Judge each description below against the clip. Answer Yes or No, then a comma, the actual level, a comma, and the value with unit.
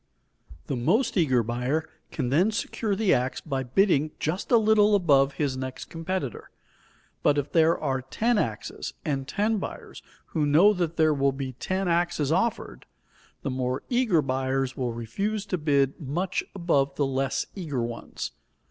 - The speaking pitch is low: No, medium, 150 Hz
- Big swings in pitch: Yes, wide, 5.9 semitones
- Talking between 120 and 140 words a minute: No, average, 160 wpm